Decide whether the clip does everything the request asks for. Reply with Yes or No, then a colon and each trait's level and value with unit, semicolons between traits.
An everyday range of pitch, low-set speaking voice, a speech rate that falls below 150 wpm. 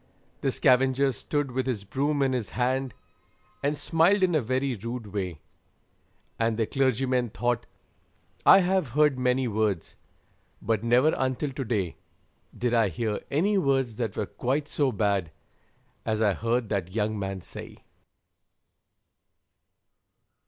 Yes: average, 4.0 semitones; low, 125 Hz; average, 140 wpm